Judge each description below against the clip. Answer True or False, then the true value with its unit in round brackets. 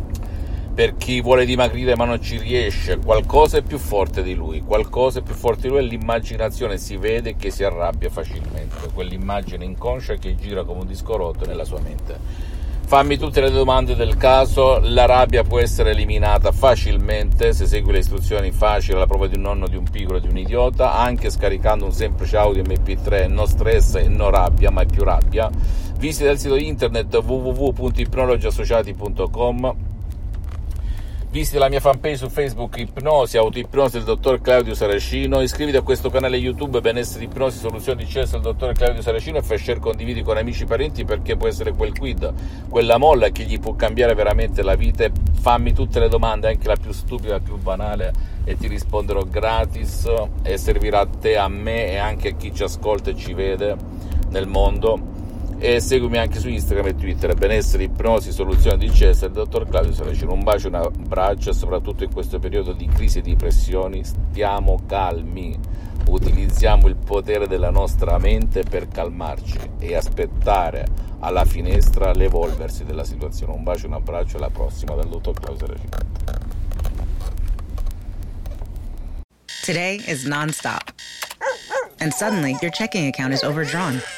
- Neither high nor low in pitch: False (95 Hz)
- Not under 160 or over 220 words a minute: True (165 wpm)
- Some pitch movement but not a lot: False (5.8 semitones)